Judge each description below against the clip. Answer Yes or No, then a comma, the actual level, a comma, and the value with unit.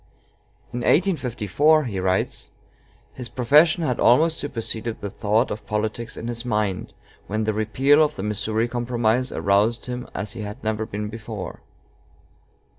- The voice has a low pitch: Yes, low, 115 Hz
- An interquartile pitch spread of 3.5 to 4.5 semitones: No, average, 2.9 semitones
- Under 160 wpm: Yes, average, 145 wpm